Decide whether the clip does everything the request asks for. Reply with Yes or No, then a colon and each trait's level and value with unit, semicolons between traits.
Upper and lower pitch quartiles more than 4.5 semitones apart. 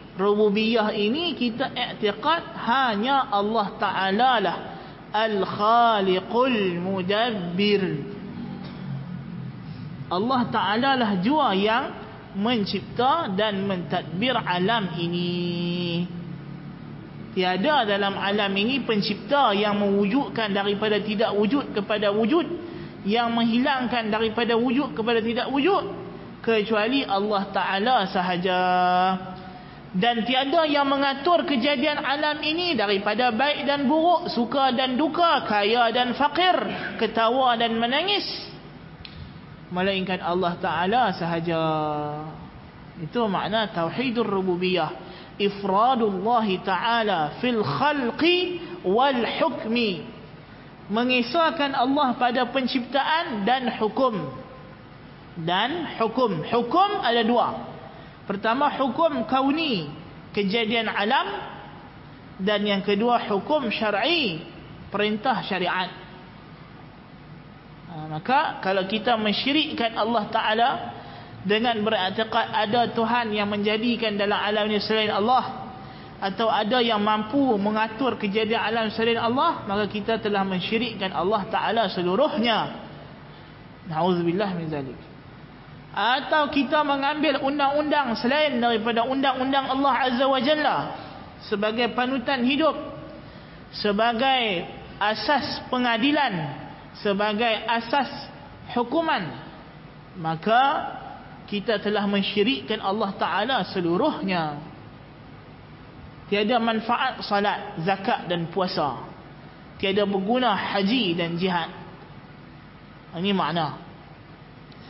Yes: average, 5.0 semitones